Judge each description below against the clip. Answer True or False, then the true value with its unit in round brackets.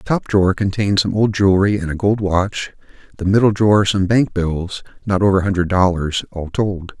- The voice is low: True (95 Hz)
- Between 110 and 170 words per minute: False (205 wpm)